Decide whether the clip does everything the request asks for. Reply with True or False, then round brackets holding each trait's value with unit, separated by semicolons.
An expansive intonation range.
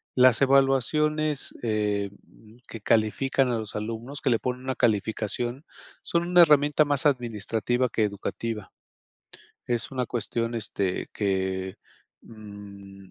False (4.2 semitones)